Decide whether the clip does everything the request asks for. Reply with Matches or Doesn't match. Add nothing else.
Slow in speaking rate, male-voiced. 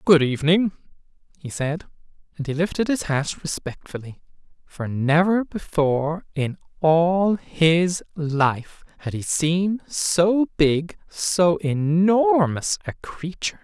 Matches